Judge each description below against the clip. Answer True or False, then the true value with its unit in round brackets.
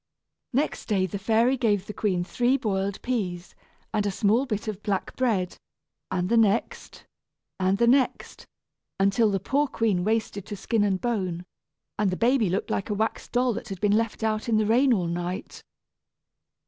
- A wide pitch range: False (3.4 semitones)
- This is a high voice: True (210 Hz)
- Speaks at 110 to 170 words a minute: False (180 wpm)